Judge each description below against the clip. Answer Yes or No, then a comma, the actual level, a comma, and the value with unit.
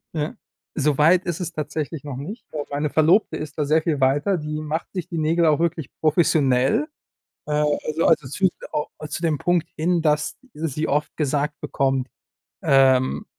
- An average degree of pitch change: No, narrow, 2.1 semitones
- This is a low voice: No, medium, 150 Hz